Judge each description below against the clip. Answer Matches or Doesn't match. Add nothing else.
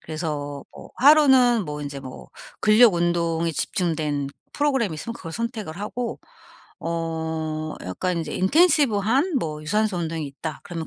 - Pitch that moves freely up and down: Matches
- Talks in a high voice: Doesn't match